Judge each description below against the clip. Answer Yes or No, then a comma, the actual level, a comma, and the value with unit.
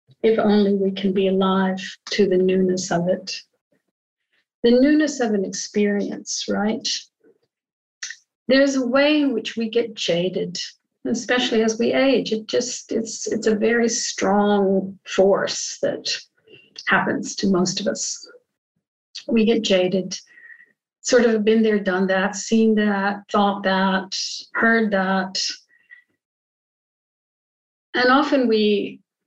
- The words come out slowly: Yes, slow, 125 wpm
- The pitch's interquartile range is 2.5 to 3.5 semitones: No, average, 4.3 semitones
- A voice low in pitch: No, high, 220 Hz